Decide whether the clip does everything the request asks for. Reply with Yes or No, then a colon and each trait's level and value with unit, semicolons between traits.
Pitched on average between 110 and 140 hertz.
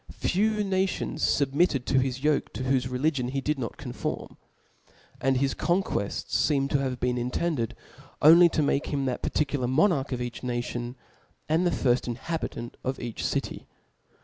Yes: low, 135 Hz